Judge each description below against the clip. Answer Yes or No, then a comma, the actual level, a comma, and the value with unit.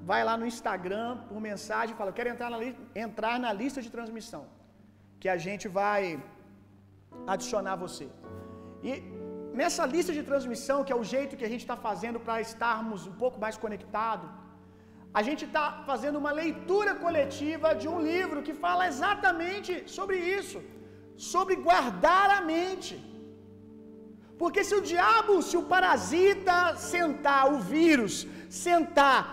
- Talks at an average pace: No, fast, 155 wpm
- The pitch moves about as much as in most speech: No, wide, 8.1 semitones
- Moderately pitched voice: No, very high, 265 Hz